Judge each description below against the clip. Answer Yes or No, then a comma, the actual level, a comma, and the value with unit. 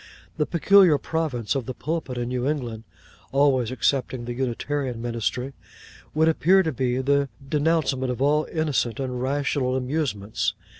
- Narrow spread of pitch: No, average, 3.3 semitones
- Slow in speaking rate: No, average, 145 wpm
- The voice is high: No, low, 135 Hz